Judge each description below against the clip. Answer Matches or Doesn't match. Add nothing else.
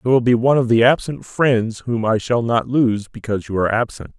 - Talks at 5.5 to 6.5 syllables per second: Matches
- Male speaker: Matches